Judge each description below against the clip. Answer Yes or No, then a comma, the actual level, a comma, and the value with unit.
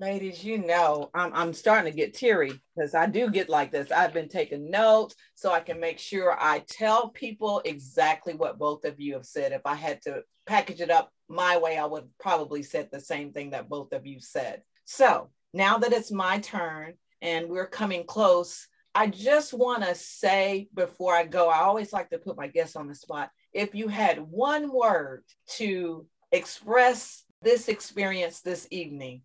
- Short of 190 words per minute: No, average, 195 wpm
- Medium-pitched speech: Yes, medium, 180 Hz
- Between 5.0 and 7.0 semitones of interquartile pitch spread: Yes, average, 5.3 semitones